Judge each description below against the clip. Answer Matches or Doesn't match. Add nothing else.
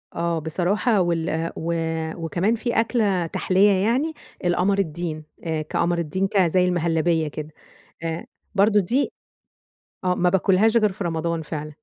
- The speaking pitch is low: Doesn't match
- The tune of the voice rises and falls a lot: Doesn't match